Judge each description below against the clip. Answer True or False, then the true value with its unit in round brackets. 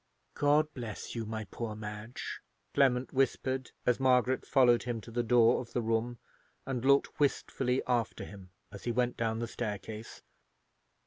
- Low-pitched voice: True (120 Hz)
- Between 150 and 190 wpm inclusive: True (155 wpm)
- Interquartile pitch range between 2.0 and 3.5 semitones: True (2.5 semitones)